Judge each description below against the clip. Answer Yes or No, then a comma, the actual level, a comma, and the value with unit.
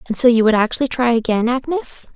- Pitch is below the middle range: No, high, 245 Hz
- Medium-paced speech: No, fast, 225 wpm